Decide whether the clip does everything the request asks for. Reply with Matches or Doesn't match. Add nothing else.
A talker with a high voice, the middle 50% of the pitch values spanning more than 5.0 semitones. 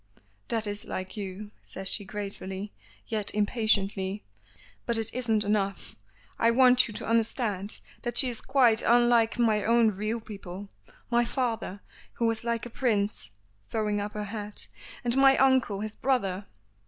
Doesn't match